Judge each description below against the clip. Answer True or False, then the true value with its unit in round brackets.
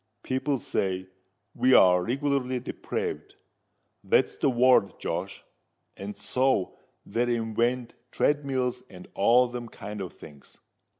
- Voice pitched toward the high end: False (120 Hz)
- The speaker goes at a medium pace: False (100 wpm)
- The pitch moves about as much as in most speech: True (4.3 semitones)